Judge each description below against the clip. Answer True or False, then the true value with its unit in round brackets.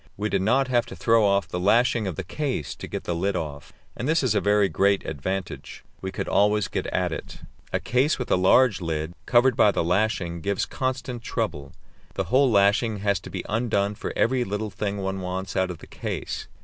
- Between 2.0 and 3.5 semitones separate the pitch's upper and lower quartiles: False (4.0 semitones)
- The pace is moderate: False (215 wpm)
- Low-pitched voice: True (100 Hz)